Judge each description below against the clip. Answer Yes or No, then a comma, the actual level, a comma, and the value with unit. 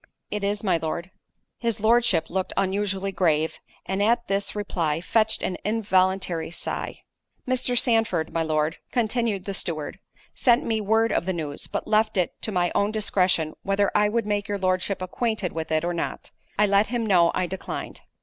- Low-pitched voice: No, high, 195 Hz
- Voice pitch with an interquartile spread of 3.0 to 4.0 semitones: Yes, average, 3.6 semitones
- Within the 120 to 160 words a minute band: No, average, 180 wpm